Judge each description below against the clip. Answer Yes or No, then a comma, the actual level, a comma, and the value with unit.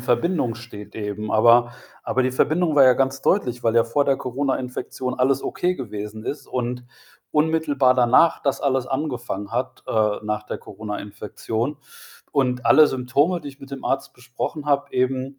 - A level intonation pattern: No, average, 3.1 semitones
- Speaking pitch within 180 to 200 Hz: No, low, 125 Hz